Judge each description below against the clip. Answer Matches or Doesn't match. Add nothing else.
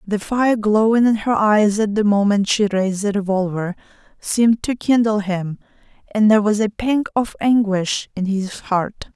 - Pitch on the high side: Matches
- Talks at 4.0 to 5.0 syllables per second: Matches